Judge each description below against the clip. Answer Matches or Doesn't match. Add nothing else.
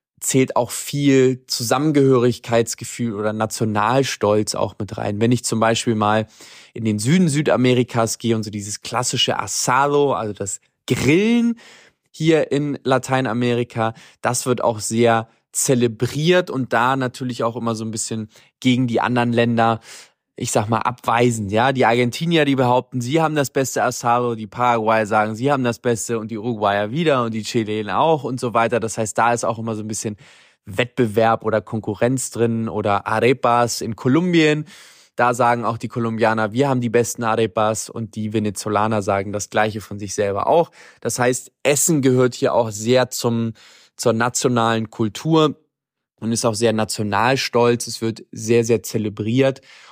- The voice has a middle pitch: Doesn't match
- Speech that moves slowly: Doesn't match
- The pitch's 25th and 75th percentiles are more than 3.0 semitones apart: Doesn't match